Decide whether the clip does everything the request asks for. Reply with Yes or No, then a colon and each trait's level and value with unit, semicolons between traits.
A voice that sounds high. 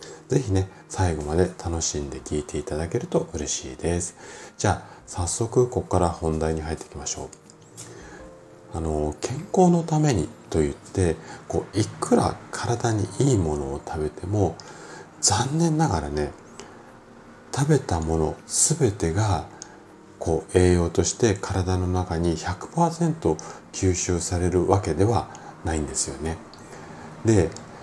No: very low, 90 Hz